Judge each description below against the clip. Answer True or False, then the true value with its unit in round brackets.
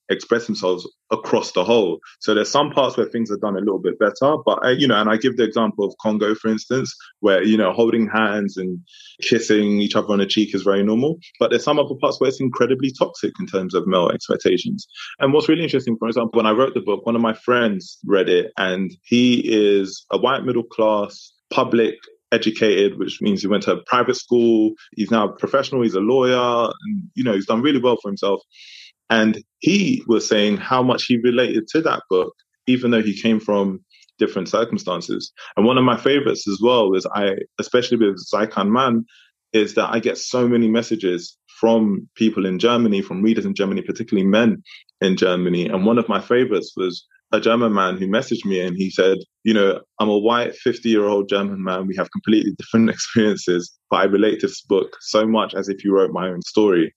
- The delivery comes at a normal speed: False (215 wpm)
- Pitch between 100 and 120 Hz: True (110 Hz)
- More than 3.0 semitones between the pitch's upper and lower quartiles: True (3.7 semitones)